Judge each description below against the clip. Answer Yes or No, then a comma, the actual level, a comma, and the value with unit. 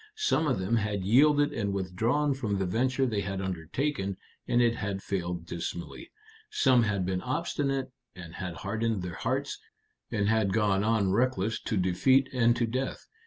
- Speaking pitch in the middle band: No, low, 110 Hz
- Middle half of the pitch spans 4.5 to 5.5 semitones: Yes, average, 5.2 semitones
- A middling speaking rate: Yes, average, 165 wpm